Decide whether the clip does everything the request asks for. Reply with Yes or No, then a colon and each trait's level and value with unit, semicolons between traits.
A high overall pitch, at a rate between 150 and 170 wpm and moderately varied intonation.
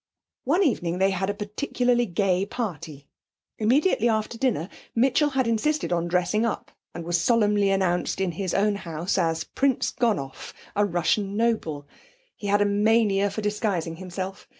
Yes: high, 205 Hz; average, 155 wpm; average, 4.5 semitones